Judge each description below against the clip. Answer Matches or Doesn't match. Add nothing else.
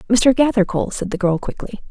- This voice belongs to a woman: Matches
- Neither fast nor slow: Matches